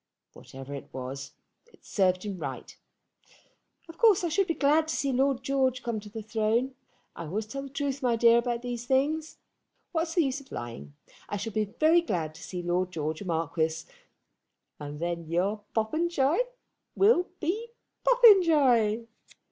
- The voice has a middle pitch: No, high, 235 Hz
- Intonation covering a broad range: Yes, wide, 9.0 semitones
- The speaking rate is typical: Yes, average, 170 wpm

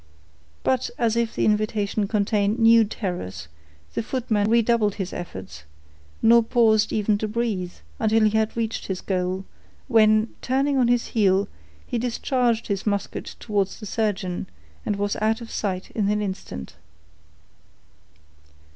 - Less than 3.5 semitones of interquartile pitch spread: Yes, narrow, 2.4 semitones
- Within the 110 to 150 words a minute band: Yes, average, 140 wpm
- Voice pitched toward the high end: Yes, high, 215 Hz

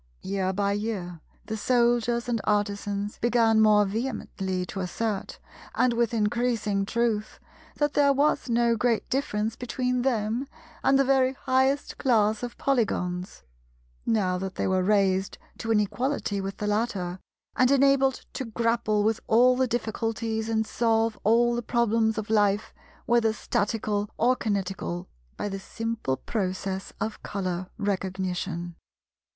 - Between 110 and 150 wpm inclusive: Yes, slow, 135 wpm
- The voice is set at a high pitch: Yes, high, 220 Hz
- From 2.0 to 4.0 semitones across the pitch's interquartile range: Yes, average, 3.1 semitones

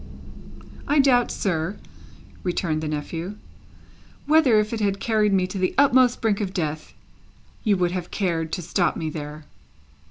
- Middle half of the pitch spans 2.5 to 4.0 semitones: No, average, 5.0 semitones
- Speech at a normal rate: Yes, average, 155 wpm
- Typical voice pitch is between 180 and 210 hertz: Yes, high, 190 Hz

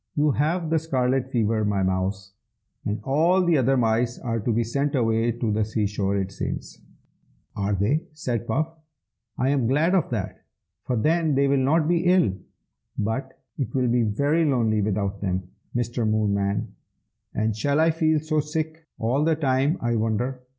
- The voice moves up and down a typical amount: No, wide, 5.8 semitones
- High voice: No, low, 125 Hz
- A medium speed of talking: Yes, average, 175 wpm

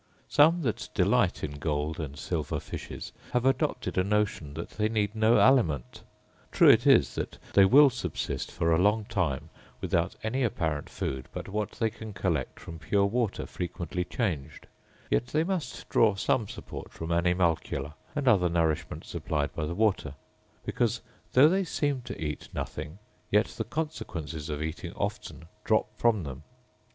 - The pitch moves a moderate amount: No, wide, 6.3 semitones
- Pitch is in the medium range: No, very low, 95 Hz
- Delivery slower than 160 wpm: No, average, 165 wpm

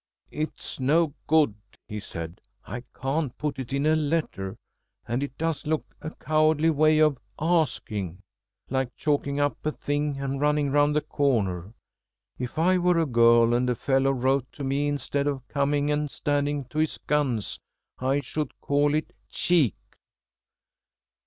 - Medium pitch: Yes, medium, 145 Hz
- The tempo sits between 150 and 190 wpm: Yes, average, 155 wpm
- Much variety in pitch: No, average, 2.9 semitones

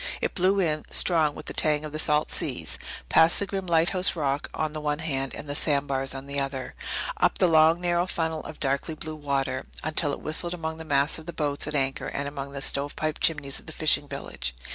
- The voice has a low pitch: No, medium, 150 Hz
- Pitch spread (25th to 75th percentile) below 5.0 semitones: Yes, narrow, 2.5 semitones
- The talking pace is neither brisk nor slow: No, fast, 225 wpm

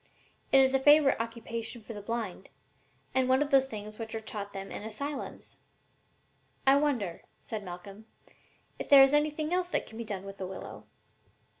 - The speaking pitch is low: No, high, 230 Hz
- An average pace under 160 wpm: No, average, 180 wpm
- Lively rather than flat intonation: No, average, 4.7 semitones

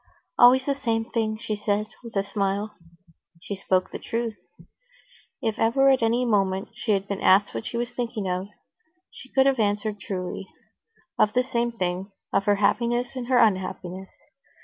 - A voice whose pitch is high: Yes, high, 215 Hz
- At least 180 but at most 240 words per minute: No, average, 170 wpm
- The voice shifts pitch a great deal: No, average, 3.3 semitones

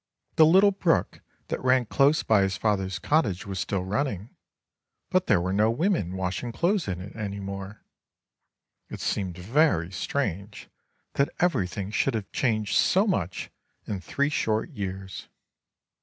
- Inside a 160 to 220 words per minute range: No, average, 145 wpm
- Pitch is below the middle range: Yes, low, 105 Hz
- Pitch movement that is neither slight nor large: No, wide, 6.6 semitones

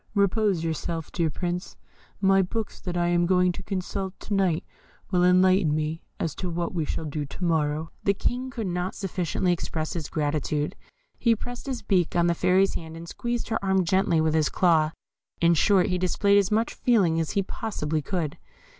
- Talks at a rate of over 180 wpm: Yes, average, 190 wpm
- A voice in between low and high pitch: Yes, medium, 180 Hz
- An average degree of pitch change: Yes, average, 3.3 semitones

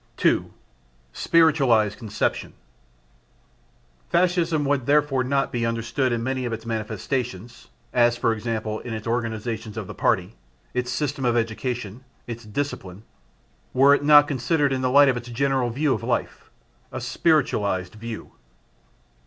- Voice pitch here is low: Yes, low, 120 Hz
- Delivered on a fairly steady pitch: No, average, 3.5 semitones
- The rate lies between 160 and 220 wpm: No, average, 140 wpm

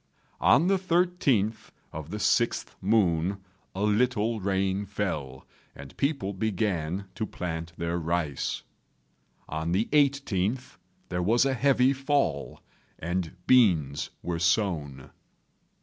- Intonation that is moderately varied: No, wide, 6.5 semitones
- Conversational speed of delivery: No, slow, 115 wpm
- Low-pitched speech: Yes, low, 100 Hz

